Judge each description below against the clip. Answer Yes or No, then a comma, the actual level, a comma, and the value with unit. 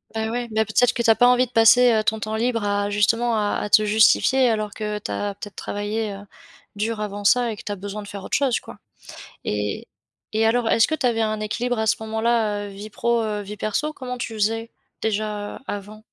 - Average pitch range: No, narrow, 2.1 semitones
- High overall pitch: Yes, high, 220 Hz